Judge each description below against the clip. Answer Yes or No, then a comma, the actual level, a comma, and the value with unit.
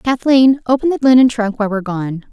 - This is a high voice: Yes, high, 235 Hz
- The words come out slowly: No, fast, 205 wpm